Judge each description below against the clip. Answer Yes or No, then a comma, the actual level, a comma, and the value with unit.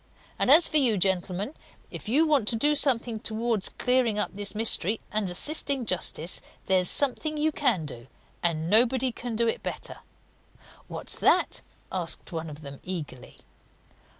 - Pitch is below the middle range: No, high, 220 Hz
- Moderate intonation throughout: No, wide, 6.1 semitones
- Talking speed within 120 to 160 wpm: Yes, average, 155 wpm